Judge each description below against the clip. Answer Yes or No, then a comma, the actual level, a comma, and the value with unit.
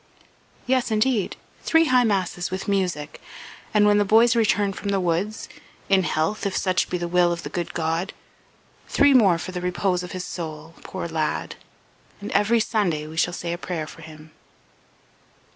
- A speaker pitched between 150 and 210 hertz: Yes, medium, 185 Hz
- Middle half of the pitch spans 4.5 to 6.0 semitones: No, average, 3.5 semitones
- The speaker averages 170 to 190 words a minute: Yes, average, 175 wpm